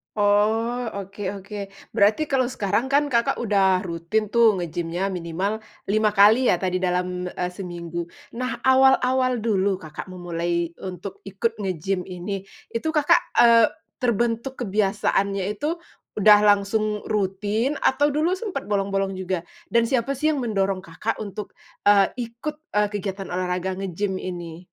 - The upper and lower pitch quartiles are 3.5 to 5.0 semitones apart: Yes, average, 4.1 semitones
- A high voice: Yes, high, 205 Hz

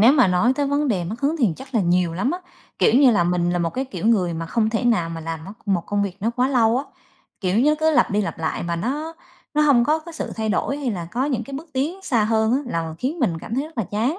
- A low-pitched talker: No, high, 230 Hz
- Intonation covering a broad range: Yes, wide, 7.2 semitones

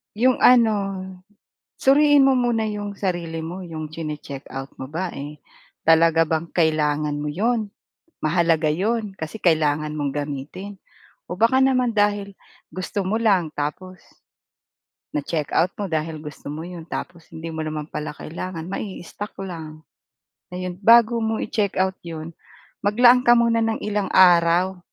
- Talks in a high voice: No, medium, 180 Hz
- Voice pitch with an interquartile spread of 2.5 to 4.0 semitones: No, average, 5.1 semitones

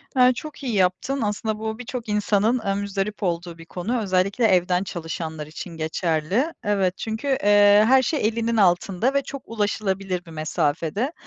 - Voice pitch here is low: No, high, 205 Hz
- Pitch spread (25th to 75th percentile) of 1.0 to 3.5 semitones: No, average, 4.3 semitones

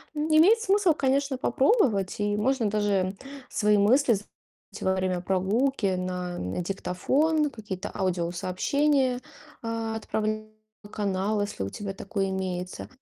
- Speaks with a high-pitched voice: Yes, high, 210 Hz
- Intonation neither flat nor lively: No, wide, 5.9 semitones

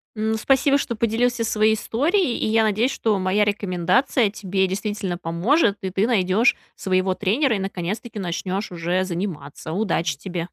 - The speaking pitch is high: Yes, high, 205 Hz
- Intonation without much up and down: No, average, 3.4 semitones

